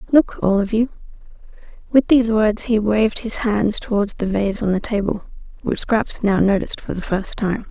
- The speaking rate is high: No, average, 195 wpm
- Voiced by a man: No, female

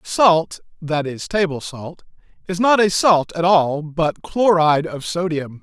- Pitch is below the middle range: No, medium, 165 Hz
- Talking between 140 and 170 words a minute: Yes, average, 160 wpm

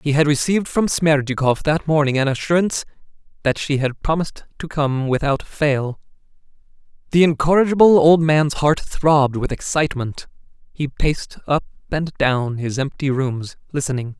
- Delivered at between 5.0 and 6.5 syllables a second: Yes, 5.1 syllables/s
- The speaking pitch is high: No, medium, 145 Hz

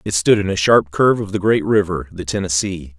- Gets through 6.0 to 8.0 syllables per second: No, 5.6 syllables/s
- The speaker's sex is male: Yes, male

